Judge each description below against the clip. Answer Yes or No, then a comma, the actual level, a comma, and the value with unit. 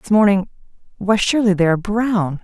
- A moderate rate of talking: Yes, average, 150 wpm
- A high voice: Yes, high, 200 Hz